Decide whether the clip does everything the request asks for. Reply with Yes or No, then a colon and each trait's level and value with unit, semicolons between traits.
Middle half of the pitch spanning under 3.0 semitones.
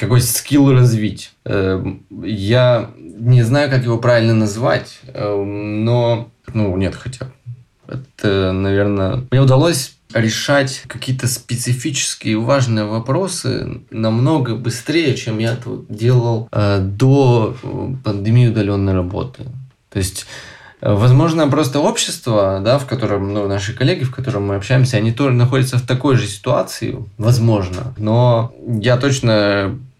No: average, 3.4 semitones